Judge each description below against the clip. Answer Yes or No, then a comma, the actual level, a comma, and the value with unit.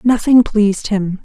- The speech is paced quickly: No, average, 145 wpm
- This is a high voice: Yes, high, 210 Hz